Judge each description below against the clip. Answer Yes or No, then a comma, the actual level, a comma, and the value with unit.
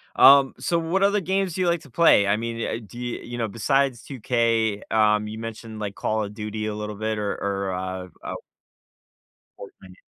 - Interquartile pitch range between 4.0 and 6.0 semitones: Yes, average, 4.7 semitones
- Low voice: Yes, low, 115 Hz